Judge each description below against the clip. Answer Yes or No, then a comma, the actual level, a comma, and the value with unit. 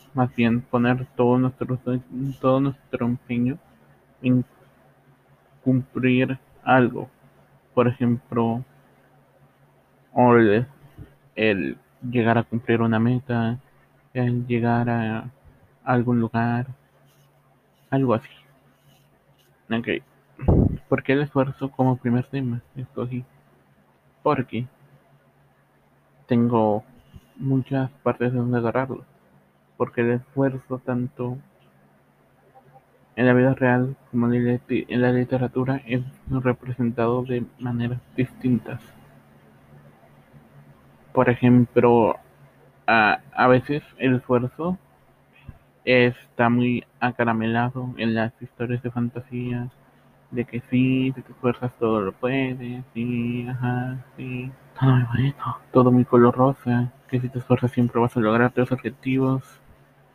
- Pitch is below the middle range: Yes, low, 125 Hz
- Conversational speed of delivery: No, slow, 105 wpm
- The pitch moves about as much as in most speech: No, narrow, 1.5 semitones